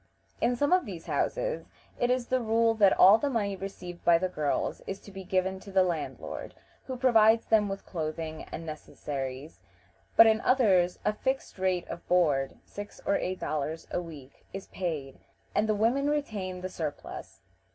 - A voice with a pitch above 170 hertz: Yes, high, 190 Hz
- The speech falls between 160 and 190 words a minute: Yes, average, 180 wpm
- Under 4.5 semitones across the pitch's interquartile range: No, average, 5.1 semitones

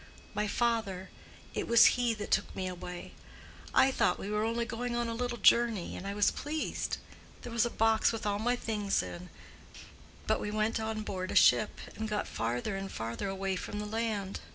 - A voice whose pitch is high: Yes, high, 215 Hz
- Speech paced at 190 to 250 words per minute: Yes, average, 200 wpm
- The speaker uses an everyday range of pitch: Yes, average, 3.1 semitones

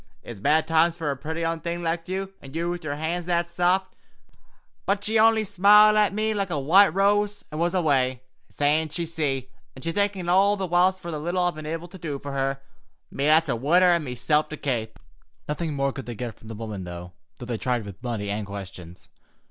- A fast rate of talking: Yes, fast, 225 wpm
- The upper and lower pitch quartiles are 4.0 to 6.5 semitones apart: Yes, average, 5.2 semitones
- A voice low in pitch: No, medium, 160 Hz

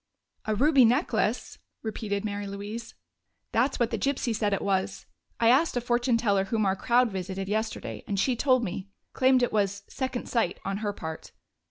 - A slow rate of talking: No, average, 180 wpm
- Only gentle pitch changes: No, average, 3.6 semitones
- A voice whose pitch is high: Yes, high, 220 Hz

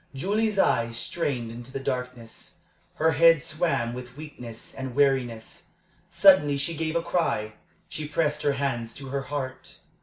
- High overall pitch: No, medium, 140 Hz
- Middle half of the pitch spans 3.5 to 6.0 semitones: Yes, average, 4.5 semitones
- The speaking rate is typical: Yes, average, 150 wpm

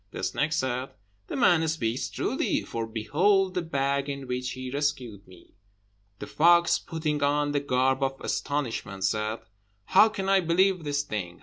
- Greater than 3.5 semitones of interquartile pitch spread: Yes, average, 4.5 semitones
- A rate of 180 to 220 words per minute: No, average, 165 wpm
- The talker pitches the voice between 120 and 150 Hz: Yes, medium, 140 Hz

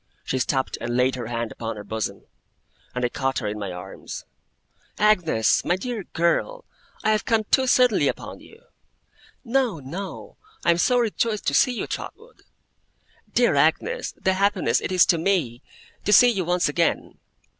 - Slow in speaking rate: No, average, 170 wpm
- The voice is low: No, medium, 175 Hz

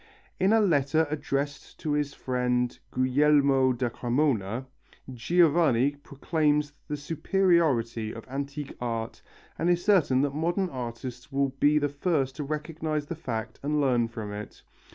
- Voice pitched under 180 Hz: Yes, medium, 140 Hz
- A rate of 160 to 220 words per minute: No, average, 140 wpm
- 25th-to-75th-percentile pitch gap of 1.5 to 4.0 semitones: Yes, average, 3.6 semitones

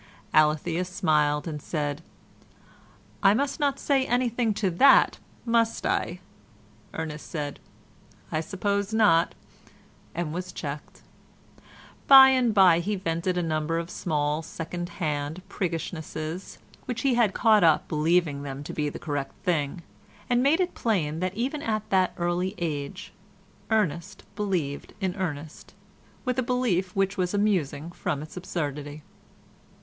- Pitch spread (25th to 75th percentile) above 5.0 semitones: Yes, wide, 5.4 semitones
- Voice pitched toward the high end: No, medium, 175 Hz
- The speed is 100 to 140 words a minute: Yes, slow, 135 wpm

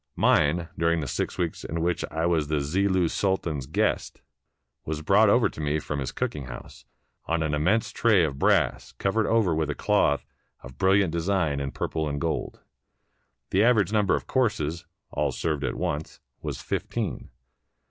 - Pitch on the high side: No, very low, 80 Hz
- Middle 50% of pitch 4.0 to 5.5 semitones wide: Yes, average, 4.6 semitones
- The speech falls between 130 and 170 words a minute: No, average, 180 wpm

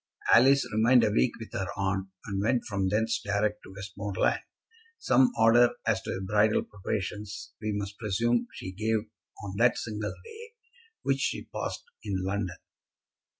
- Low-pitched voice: Yes, low, 105 Hz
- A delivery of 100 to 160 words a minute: Yes, average, 150 wpm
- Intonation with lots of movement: No, narrow, 2.6 semitones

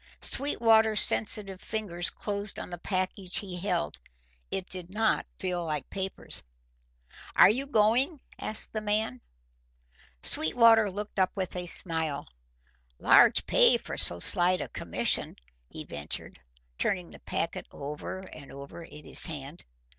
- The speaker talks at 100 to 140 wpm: Yes, slow, 135 wpm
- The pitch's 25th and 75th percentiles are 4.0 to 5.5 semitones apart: Yes, average, 4.3 semitones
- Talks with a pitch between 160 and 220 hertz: Yes, medium, 185 Hz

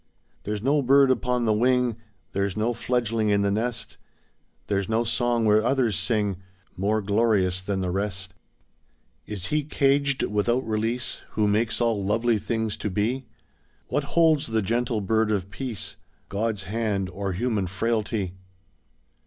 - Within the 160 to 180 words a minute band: No, average, 145 wpm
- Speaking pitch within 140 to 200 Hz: No, low, 110 Hz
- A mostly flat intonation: No, average, 3.1 semitones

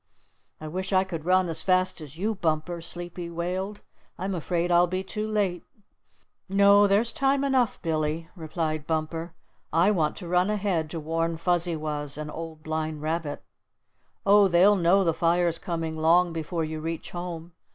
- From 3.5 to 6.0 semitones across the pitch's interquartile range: No, average, 2.8 semitones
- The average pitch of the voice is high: No, medium, 170 Hz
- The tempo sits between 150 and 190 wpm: Yes, average, 165 wpm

